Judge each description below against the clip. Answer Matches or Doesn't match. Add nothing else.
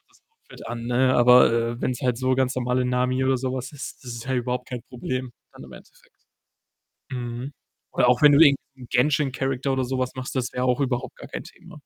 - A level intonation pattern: Matches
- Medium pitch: Doesn't match